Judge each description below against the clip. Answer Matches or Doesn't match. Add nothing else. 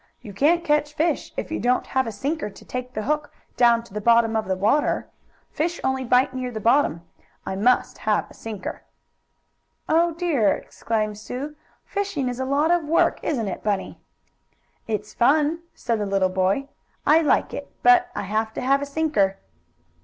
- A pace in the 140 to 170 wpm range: Doesn't match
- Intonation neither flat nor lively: Doesn't match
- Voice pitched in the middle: Doesn't match